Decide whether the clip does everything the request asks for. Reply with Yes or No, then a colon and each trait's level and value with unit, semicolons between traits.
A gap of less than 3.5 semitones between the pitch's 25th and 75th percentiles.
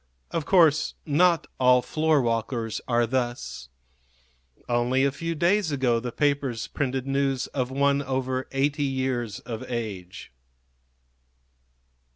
Yes: average, 2.9 semitones